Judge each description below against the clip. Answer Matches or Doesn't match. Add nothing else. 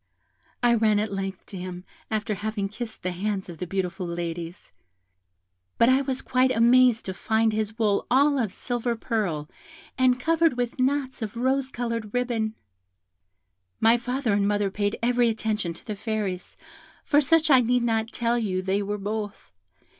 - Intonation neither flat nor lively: Matches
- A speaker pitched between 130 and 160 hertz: Doesn't match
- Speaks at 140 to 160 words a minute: Doesn't match